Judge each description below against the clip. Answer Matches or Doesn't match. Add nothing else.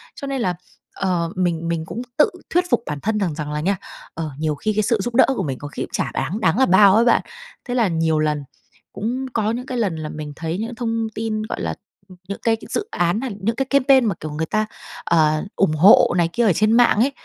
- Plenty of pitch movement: Matches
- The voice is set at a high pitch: Matches